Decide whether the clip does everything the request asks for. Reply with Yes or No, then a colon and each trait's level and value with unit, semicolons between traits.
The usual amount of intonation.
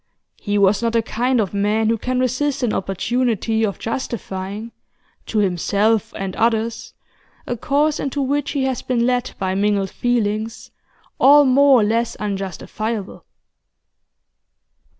Yes: average, 3.7 semitones